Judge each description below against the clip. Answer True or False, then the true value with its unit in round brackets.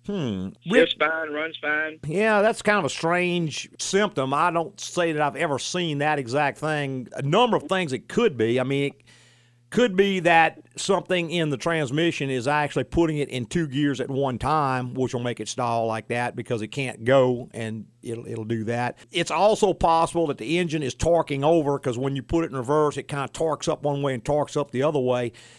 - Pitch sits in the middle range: True (145 Hz)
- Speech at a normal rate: False (215 wpm)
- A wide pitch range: False (4.7 semitones)